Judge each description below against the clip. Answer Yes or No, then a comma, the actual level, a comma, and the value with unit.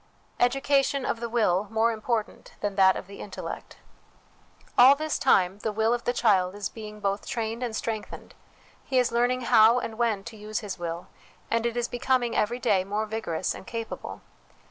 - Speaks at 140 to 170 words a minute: No, average, 185 wpm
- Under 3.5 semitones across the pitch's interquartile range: Yes, average, 2.8 semitones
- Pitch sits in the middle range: No, high, 225 Hz